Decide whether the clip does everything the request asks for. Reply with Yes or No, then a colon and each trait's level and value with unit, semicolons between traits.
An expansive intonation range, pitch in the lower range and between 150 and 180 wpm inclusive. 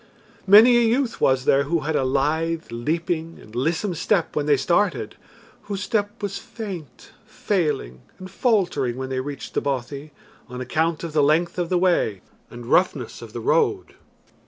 No: wide, 6.3 semitones; medium, 165 Hz; average, 170 wpm